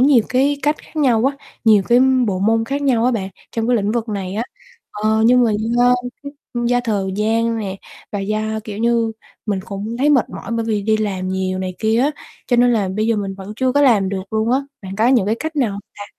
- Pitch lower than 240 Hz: Yes, high, 225 Hz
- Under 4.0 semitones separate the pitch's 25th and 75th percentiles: Yes, average, 3.3 semitones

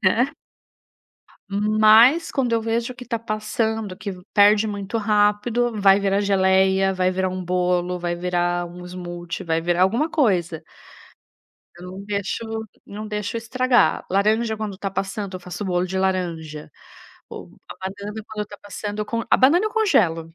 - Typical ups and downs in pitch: Yes, average, 3.3 semitones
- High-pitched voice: Yes, high, 200 Hz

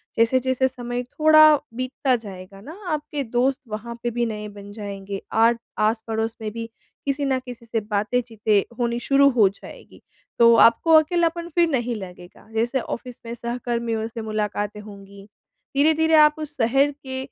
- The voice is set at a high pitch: Yes, high, 235 Hz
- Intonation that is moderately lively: Yes, average, 3.8 semitones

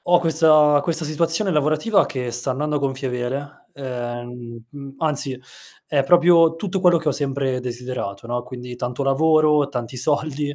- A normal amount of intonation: Yes, average, 3.7 semitones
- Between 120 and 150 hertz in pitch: Yes, medium, 140 Hz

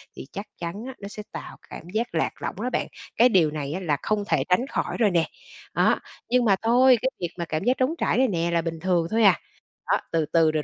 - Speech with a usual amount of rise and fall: No, wide, 6.0 semitones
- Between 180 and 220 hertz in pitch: Yes, high, 190 Hz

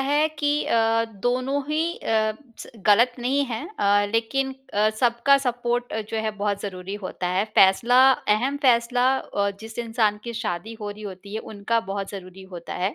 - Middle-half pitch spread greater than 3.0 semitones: Yes, average, 3.4 semitones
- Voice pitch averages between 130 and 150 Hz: No, high, 225 Hz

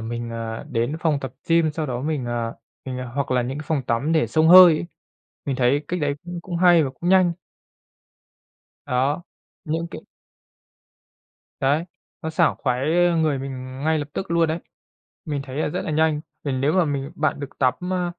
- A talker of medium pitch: Yes, medium, 145 Hz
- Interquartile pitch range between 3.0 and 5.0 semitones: Yes, average, 3.7 semitones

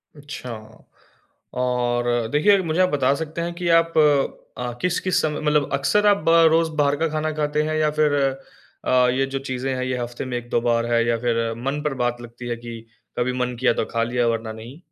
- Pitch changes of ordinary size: Yes, average, 4.2 semitones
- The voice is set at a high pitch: No, low, 130 Hz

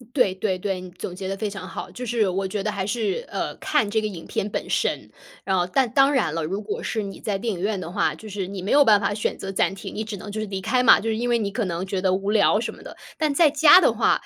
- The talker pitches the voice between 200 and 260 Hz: Yes, high, 205 Hz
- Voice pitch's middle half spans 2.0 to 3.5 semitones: Yes, average, 2.8 semitones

